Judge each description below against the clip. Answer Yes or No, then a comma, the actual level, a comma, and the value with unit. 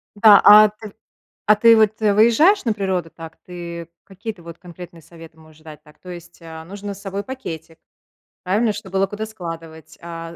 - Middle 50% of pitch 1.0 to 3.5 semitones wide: No, average, 4.1 semitones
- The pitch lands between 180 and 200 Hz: Yes, medium, 185 Hz